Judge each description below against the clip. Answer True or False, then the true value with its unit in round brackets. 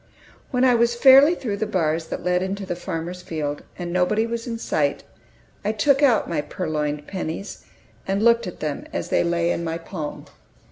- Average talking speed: True (190 wpm)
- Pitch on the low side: False (180 Hz)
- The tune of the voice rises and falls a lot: True (5.8 semitones)